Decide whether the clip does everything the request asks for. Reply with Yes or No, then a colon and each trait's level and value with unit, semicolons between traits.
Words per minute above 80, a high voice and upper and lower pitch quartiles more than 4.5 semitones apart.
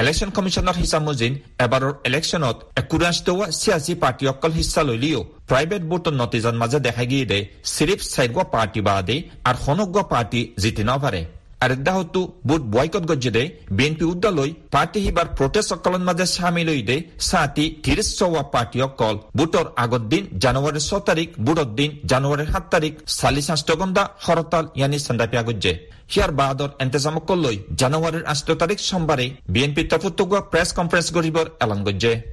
No: fast, 120 wpm; medium, 150 Hz; wide, 5.5 semitones